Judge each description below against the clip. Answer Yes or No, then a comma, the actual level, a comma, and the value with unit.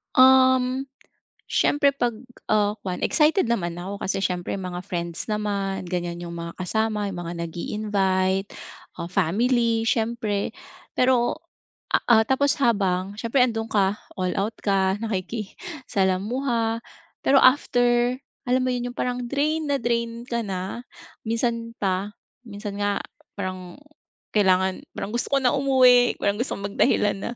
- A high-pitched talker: Yes, high, 220 Hz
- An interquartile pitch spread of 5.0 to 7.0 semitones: No, average, 4.3 semitones